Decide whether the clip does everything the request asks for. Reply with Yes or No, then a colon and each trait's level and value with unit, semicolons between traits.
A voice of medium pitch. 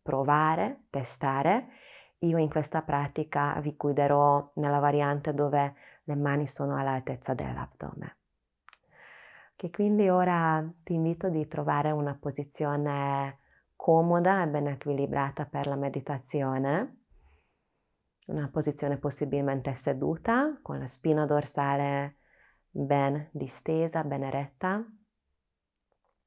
Yes: medium, 145 Hz